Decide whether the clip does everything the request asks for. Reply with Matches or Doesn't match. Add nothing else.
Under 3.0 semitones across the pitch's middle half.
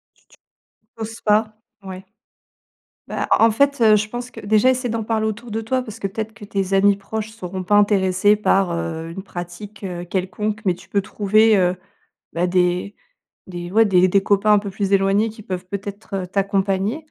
Matches